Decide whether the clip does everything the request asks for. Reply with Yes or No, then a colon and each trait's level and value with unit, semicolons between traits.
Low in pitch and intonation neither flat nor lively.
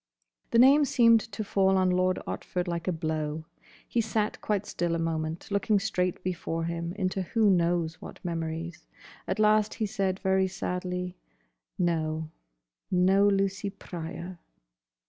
No: medium, 185 Hz; average, 3.0 semitones